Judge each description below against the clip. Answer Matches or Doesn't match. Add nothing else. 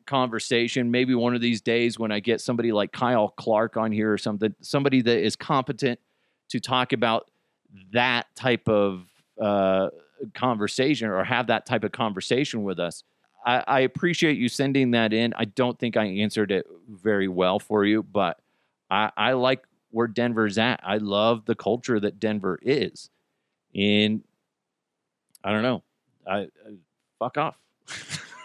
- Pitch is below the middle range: Matches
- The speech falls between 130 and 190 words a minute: Matches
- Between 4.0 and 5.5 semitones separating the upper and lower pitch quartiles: Doesn't match